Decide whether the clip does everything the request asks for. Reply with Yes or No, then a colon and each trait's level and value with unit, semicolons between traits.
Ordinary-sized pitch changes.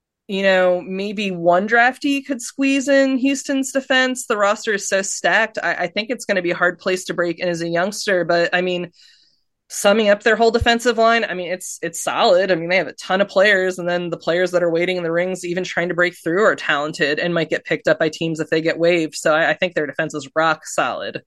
Yes: average, 4.0 semitones